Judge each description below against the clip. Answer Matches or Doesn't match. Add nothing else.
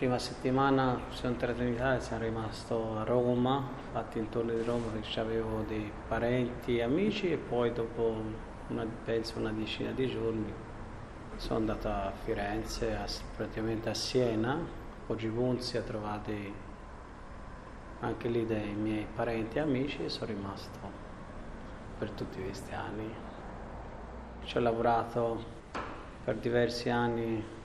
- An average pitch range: Doesn't match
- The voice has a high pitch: Doesn't match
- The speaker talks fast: Doesn't match